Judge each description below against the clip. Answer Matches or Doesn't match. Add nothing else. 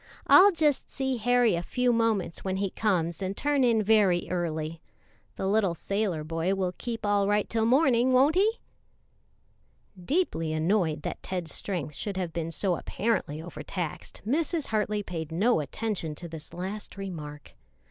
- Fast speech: Doesn't match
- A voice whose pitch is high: Matches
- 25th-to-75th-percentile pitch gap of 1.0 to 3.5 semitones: Doesn't match